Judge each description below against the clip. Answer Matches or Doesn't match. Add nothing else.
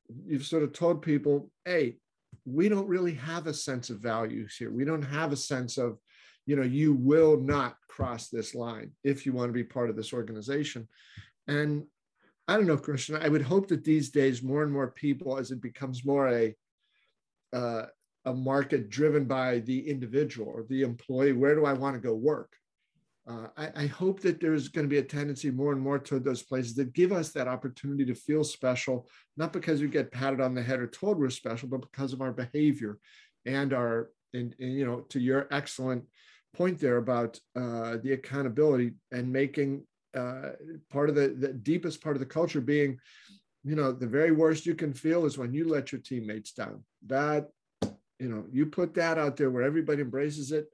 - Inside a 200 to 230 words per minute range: Matches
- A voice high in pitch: Doesn't match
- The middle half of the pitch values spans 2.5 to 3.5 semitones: Matches